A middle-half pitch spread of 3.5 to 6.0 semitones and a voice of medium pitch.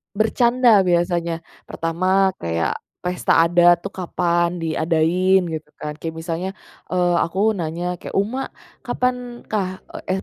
No: average, 2.7 semitones; medium, 180 Hz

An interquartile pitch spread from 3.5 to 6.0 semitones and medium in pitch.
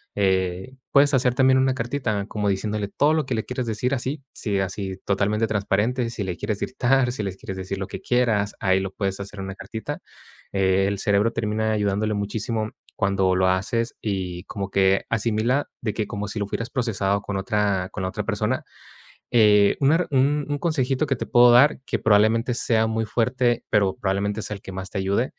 No: average, 3.8 semitones; low, 105 Hz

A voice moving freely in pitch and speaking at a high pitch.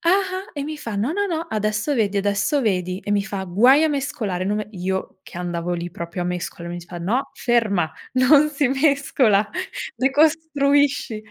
Yes: wide, 7.1 semitones; high, 220 Hz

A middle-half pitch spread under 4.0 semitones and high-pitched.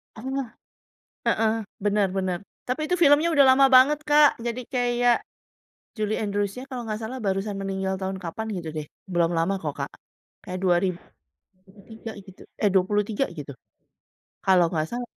No: average, 4.8 semitones; high, 205 Hz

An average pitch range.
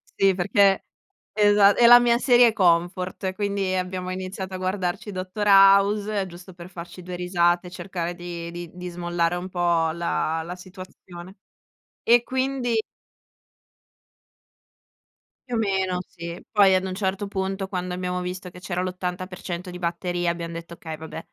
No: narrow, 2.0 semitones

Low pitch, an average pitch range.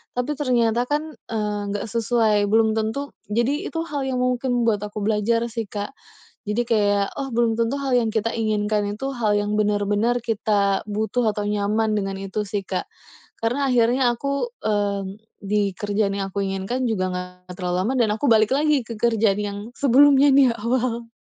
No: high, 220 Hz; average, 3.0 semitones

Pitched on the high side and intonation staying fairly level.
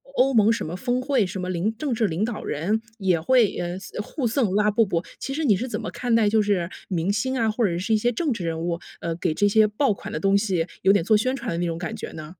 No: high, 210 Hz; average, 4.6 semitones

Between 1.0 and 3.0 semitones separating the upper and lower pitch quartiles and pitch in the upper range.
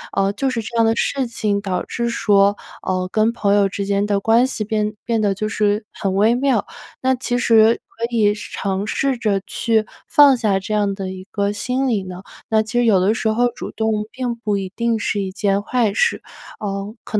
Yes: average, 2.7 semitones; high, 215 Hz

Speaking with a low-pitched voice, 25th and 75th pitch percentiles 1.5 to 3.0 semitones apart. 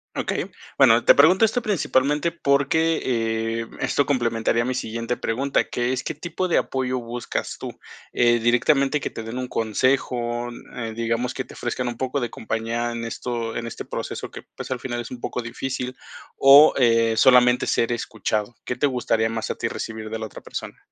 Yes: low, 120 Hz; narrow, 2.5 semitones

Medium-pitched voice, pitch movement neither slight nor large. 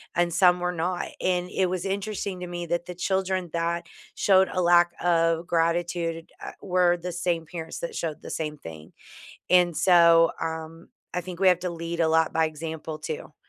No: medium, 170 Hz; narrow, 1.6 semitones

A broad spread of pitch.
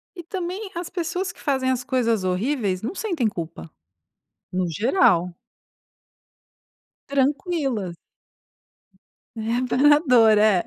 Yes: wide, 7.7 semitones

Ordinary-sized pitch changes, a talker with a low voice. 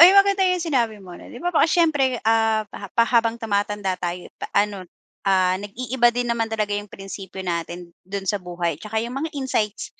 No: average, 4.2 semitones; high, 215 Hz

